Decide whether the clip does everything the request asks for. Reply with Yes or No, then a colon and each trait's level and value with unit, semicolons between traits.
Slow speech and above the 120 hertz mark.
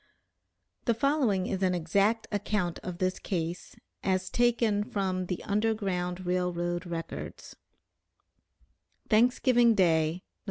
Yes: slow, 115 wpm; medium, 185 Hz